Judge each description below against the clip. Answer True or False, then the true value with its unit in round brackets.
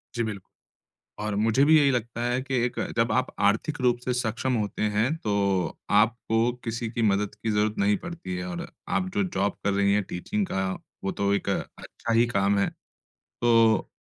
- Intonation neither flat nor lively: True (3.3 semitones)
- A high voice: False (110 Hz)